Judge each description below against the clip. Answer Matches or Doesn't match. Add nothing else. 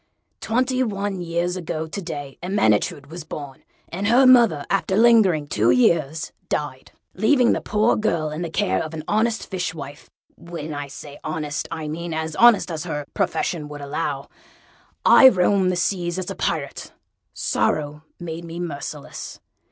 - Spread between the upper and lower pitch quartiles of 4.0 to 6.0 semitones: Matches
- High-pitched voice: Doesn't match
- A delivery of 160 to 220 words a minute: Doesn't match